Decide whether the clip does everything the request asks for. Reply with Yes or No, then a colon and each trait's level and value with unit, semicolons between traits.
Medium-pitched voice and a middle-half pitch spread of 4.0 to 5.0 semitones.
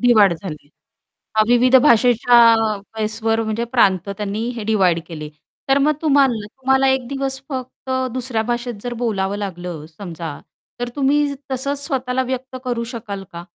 No: high, 235 Hz; average, 4.4 semitones